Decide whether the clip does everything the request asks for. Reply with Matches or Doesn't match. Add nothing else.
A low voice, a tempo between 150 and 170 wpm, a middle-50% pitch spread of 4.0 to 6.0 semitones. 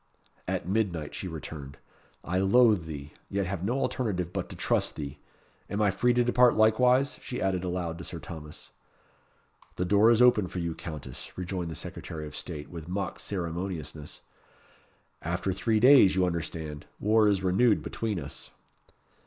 Matches